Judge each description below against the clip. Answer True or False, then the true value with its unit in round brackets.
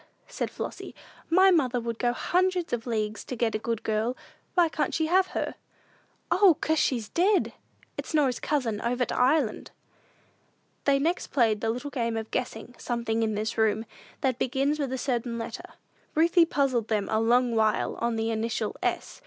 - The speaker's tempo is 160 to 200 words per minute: True (180 wpm)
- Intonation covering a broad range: False (4.8 semitones)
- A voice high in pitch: True (245 Hz)